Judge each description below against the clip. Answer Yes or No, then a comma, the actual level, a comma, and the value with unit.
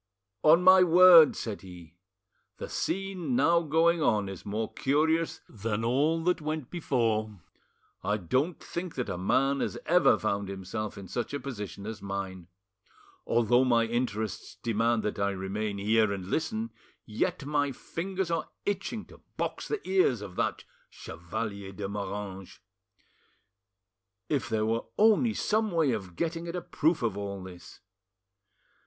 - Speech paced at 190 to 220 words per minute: No, average, 150 wpm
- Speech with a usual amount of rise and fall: No, wide, 8.5 semitones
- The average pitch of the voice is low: Yes, low, 115 Hz